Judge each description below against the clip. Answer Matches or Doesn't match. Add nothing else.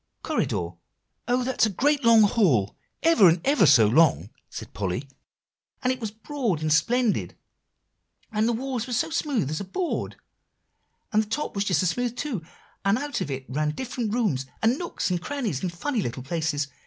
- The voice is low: Doesn't match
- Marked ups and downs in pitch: Matches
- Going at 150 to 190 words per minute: Matches